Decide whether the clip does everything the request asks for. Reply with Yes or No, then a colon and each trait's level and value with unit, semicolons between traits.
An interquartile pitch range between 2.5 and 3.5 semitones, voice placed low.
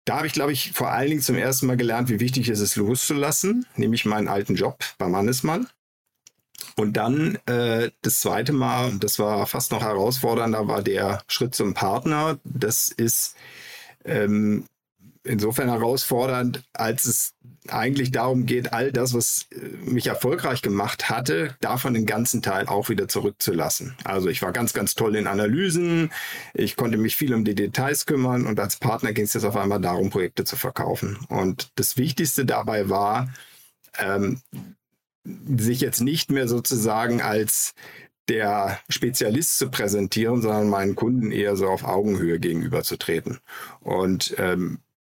No: average, 4.0 semitones; low, 120 Hz